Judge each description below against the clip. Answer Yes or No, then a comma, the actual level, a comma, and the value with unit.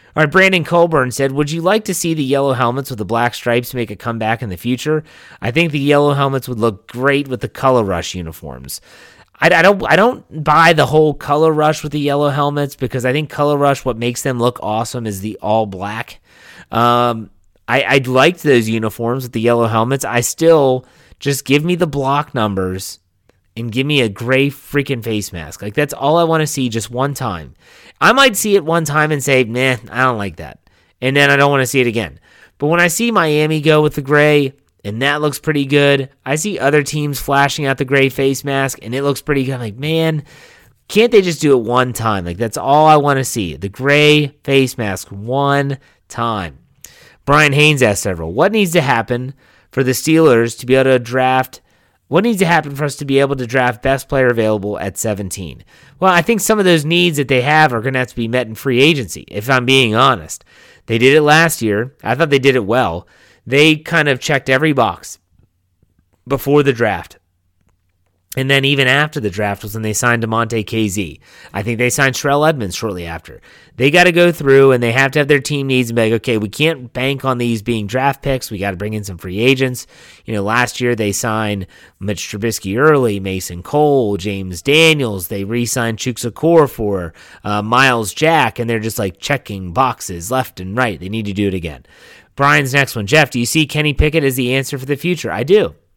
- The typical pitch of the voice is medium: No, low, 130 Hz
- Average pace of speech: No, fast, 225 wpm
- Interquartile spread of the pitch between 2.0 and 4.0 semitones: No, average, 4.8 semitones